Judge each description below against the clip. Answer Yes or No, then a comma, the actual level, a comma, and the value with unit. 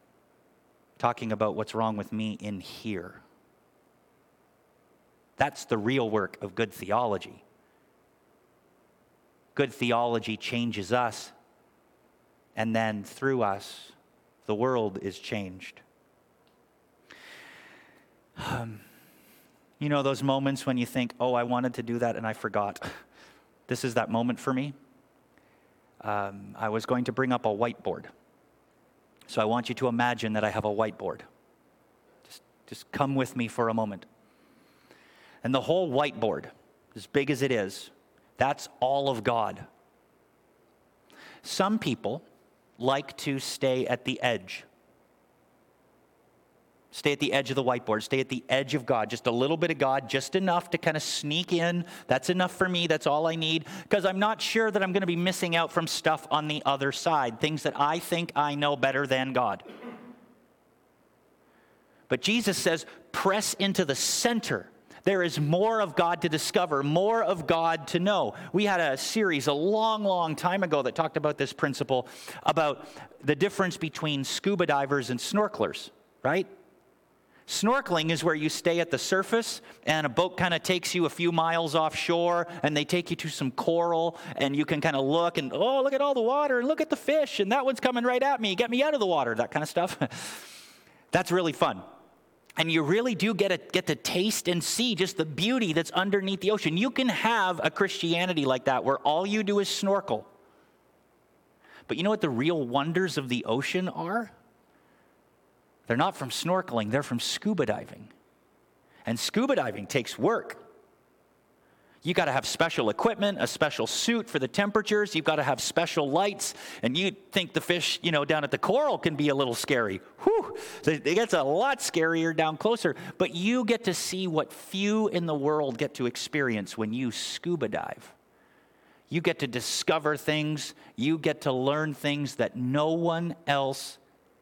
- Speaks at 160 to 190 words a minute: Yes, average, 175 wpm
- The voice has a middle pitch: Yes, medium, 160 Hz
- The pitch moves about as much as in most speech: No, wide, 6.0 semitones